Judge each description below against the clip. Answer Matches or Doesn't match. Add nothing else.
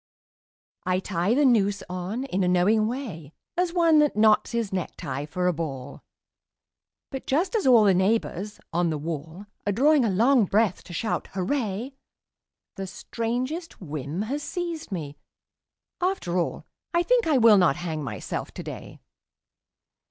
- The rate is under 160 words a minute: Matches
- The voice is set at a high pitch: Matches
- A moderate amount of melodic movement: Doesn't match